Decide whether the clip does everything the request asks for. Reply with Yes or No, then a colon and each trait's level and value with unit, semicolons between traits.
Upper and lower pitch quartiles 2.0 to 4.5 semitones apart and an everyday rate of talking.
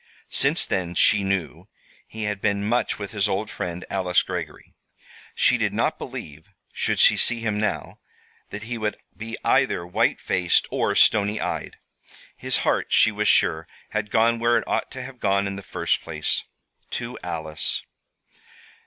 Yes: average, 3.6 semitones; average, 165 wpm